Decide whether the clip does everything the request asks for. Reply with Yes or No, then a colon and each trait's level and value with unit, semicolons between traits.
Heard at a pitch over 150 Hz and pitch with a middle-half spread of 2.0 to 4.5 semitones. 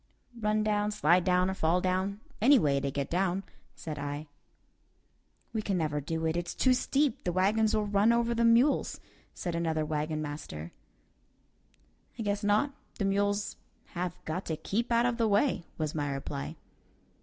No: high, 190 Hz; average, 5.2 semitones